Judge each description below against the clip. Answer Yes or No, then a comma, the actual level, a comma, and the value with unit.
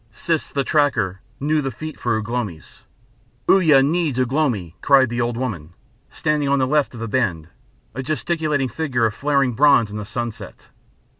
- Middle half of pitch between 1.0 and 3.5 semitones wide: No, average, 4.5 semitones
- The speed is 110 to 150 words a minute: No, average, 175 wpm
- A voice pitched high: No, low, 130 Hz